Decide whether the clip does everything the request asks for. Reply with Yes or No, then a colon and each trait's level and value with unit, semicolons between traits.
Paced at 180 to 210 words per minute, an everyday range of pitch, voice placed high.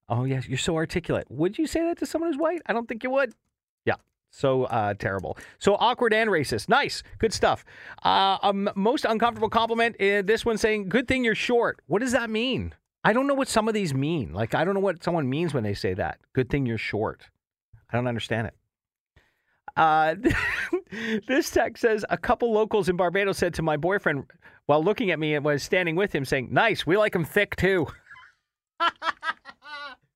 No: fast, 205 wpm; wide, 7.8 semitones; high, 205 Hz